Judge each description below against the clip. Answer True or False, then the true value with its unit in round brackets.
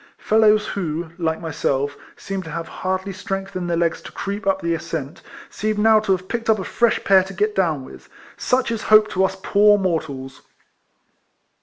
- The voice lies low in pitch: False (190 Hz)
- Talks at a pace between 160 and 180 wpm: False (190 wpm)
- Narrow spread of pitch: False (4.1 semitones)